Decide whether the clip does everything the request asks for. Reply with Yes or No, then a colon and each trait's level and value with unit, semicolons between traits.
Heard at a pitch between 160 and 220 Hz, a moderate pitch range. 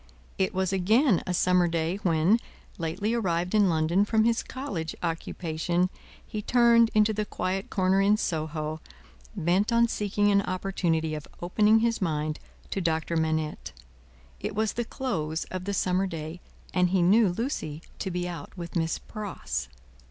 Yes: medium, 185 Hz; average, 4.3 semitones